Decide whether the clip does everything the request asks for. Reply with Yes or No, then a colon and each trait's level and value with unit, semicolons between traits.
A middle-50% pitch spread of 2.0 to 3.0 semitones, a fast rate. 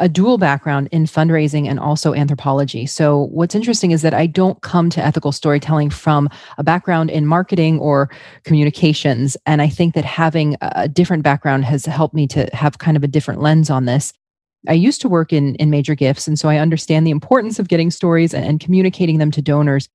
Yes: narrow, 2.4 semitones; fast, 210 wpm